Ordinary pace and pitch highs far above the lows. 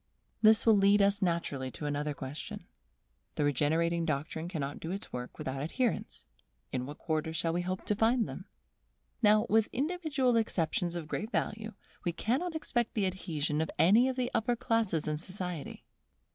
Yes: average, 170 wpm; wide, 6.4 semitones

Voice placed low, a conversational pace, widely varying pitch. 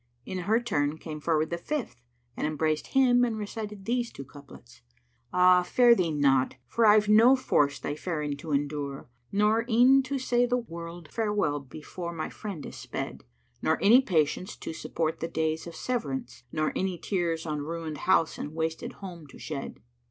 No: medium, 170 Hz; average, 180 wpm; wide, 6.2 semitones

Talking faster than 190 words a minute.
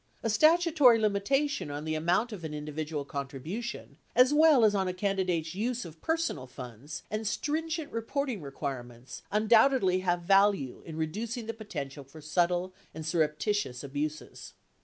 No: average, 145 wpm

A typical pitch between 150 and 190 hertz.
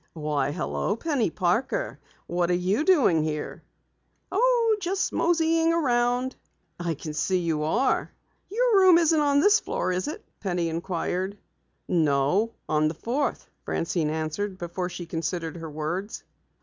Yes: medium, 185 Hz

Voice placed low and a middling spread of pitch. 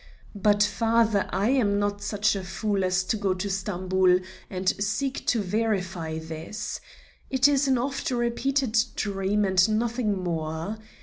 No: high, 205 Hz; average, 3.4 semitones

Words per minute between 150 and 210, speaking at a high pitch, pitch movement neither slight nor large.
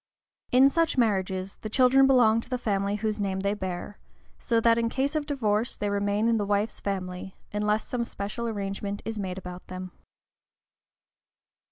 Yes: average, 170 wpm; high, 210 Hz; average, 3.0 semitones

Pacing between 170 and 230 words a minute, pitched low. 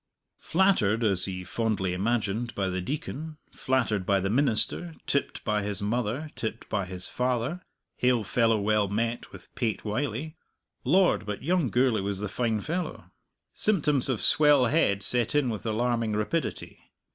No: average, 155 wpm; low, 115 Hz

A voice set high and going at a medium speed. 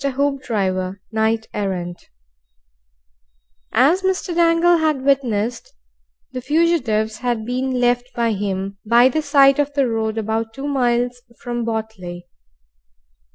No: high, 240 Hz; slow, 115 wpm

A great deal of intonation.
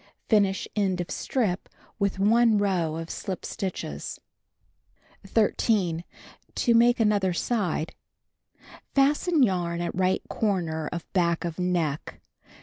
No: average, 3.9 semitones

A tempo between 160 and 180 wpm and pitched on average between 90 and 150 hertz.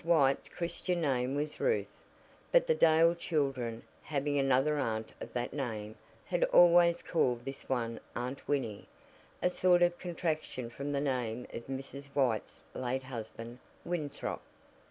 No: average, 140 wpm; medium, 140 Hz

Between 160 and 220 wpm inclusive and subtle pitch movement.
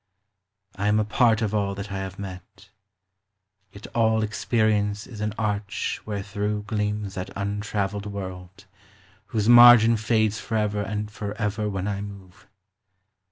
No: average, 140 wpm; narrow, 1.4 semitones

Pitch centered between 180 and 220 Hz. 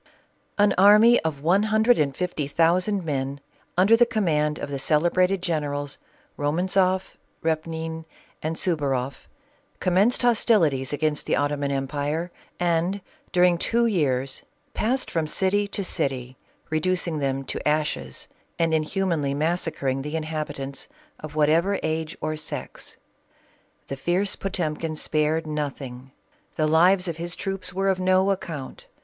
No: medium, 160 Hz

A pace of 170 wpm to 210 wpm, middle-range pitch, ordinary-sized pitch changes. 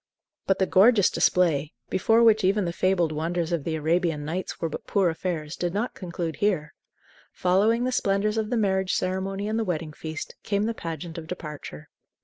Yes: average, 185 wpm; medium, 180 Hz; average, 3.8 semitones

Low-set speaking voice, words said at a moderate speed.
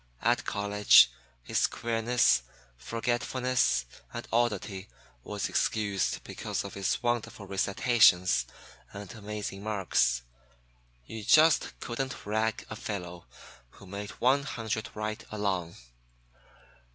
No: low, 105 Hz; slow, 105 wpm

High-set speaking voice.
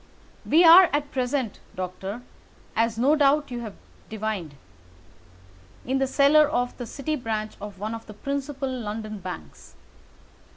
Yes: high, 230 Hz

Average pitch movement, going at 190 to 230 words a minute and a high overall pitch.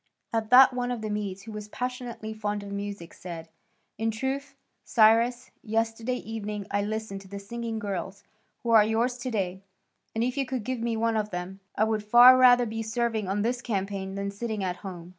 Yes: average, 3.0 semitones; average, 200 wpm; high, 220 Hz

